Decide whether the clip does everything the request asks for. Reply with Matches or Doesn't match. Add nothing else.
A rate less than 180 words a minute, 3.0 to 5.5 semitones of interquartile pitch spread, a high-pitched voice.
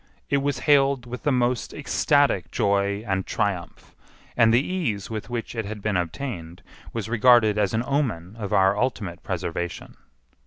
Doesn't match